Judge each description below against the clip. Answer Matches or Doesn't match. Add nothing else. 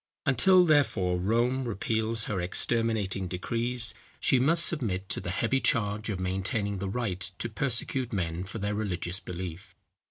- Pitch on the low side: Matches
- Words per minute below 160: Matches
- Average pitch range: Matches